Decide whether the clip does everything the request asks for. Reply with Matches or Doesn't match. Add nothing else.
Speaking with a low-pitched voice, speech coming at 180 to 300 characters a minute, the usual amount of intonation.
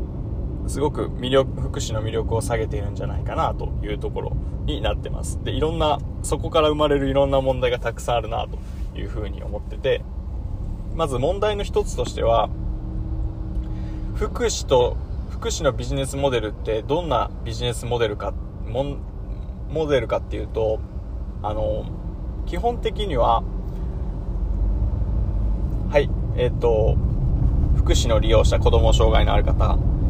Doesn't match